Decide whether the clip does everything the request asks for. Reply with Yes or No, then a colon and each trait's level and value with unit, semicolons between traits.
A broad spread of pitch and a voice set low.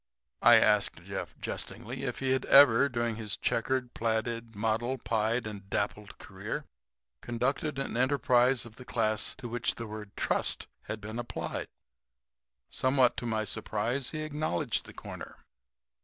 No: average, 2.9 semitones; low, 120 Hz